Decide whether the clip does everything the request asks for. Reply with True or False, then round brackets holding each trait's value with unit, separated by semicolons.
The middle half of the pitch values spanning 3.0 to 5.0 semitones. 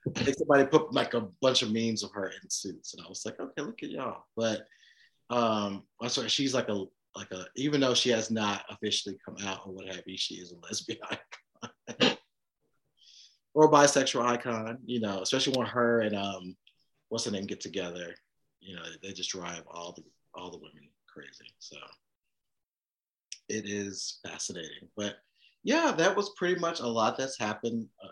True (4.6 semitones)